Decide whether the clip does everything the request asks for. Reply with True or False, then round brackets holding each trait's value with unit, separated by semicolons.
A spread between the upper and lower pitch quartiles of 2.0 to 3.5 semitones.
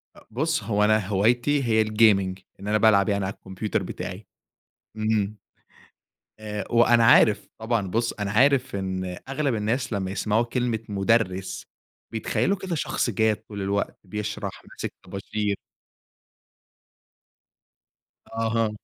True (2.7 semitones)